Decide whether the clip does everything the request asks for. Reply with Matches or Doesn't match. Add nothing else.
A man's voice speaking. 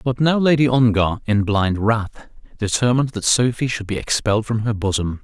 Matches